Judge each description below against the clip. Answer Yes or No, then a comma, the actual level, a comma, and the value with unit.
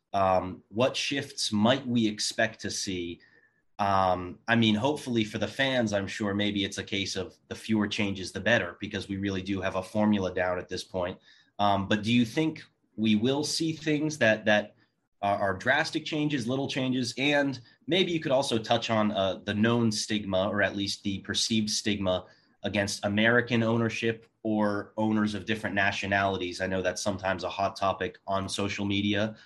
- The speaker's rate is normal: Yes, average, 185 wpm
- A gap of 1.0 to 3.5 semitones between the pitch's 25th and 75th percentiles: Yes, average, 3.1 semitones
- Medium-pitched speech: No, low, 105 Hz